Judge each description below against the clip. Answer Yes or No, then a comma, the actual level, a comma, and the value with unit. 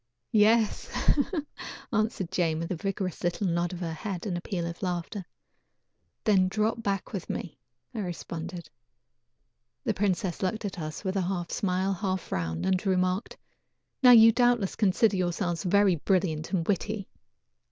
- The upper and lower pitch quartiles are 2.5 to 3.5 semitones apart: Yes, average, 2.9 semitones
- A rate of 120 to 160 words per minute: Yes, average, 150 wpm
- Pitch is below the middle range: No, medium, 185 Hz